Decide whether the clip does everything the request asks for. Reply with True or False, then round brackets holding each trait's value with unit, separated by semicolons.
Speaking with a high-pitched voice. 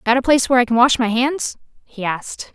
True (245 Hz)